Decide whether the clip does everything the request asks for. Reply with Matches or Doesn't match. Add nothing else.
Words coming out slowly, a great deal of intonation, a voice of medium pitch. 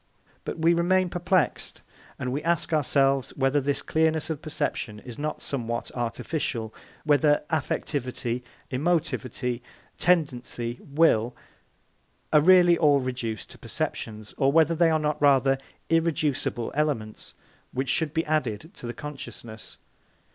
Doesn't match